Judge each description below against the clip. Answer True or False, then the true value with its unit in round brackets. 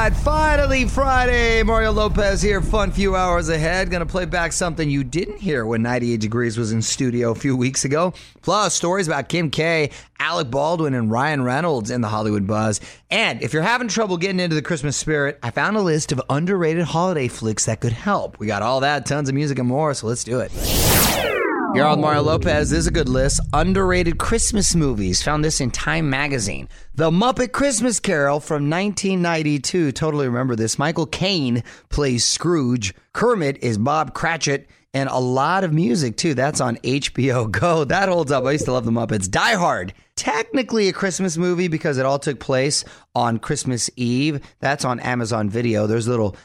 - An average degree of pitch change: False (6.1 semitones)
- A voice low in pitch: False (150 Hz)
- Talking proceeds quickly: False (190 wpm)